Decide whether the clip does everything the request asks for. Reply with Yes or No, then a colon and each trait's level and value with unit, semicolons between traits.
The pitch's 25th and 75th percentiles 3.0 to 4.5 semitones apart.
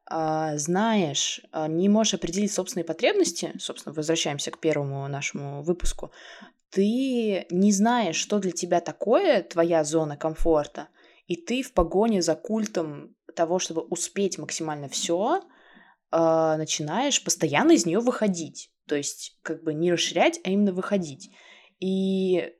Yes: average, 4.2 semitones